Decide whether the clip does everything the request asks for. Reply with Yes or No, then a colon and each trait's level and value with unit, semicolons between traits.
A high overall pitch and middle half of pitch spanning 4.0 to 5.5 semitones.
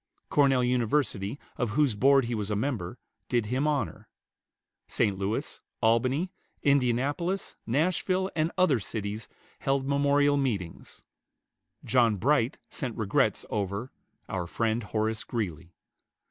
No: low, 120 Hz; average, 5.0 semitones